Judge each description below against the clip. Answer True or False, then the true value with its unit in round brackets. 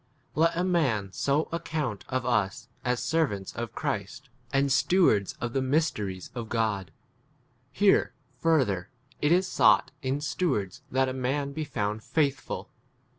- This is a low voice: True (130 Hz)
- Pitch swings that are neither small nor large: False (6.1 semitones)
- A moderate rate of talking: True (170 wpm)